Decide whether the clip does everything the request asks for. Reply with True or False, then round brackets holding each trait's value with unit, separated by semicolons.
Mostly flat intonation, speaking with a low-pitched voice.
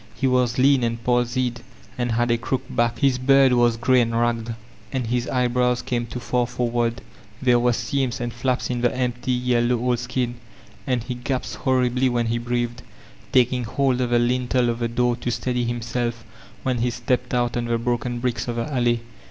True (1.0 semitones; 120 Hz)